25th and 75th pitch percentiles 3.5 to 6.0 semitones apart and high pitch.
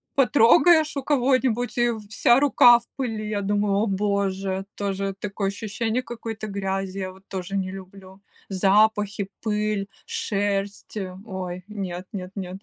No: narrow, 2.6 semitones; high, 200 Hz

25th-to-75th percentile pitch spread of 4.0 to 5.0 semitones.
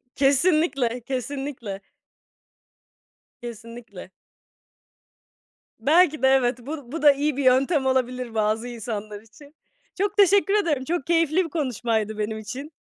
Yes: average, 4.6 semitones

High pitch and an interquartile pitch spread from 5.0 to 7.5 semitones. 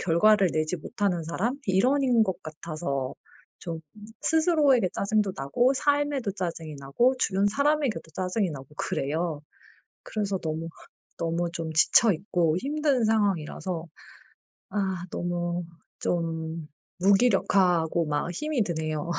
No: medium, 180 Hz; average, 5.3 semitones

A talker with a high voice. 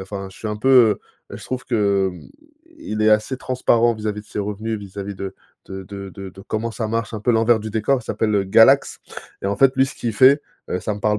No: low, 110 Hz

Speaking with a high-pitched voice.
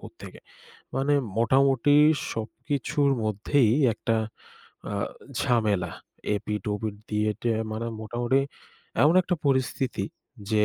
No: low, 115 Hz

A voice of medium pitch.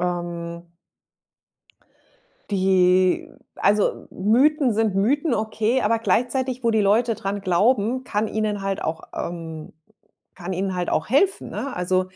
No: high, 205 Hz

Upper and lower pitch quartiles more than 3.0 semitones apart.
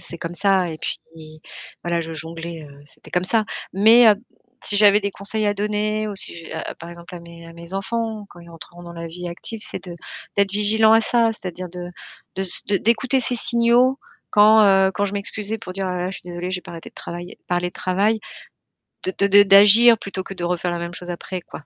Yes: average, 3.5 semitones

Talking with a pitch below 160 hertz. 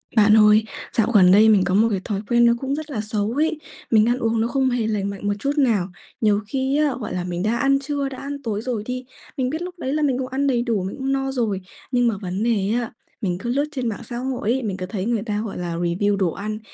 No: high, 230 Hz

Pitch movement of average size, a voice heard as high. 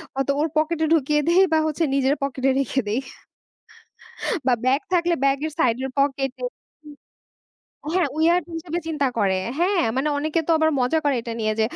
Yes: average, 3.3 semitones; very high, 285 Hz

